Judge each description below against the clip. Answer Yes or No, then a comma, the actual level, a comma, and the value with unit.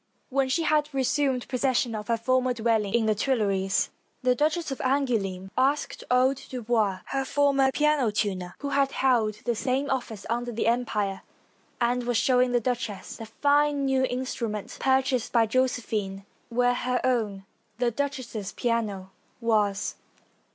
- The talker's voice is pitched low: No, high, 245 Hz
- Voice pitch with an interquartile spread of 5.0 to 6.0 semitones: No, average, 3.6 semitones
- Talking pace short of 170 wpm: Yes, average, 155 wpm